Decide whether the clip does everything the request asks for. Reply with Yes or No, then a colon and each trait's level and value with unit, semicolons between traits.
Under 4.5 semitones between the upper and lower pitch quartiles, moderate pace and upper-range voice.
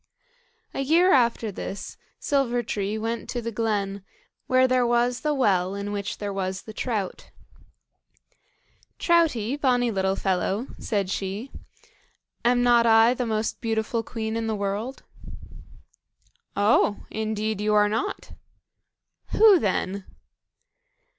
No: average, 3.2 semitones; slow, 125 wpm; high, 220 Hz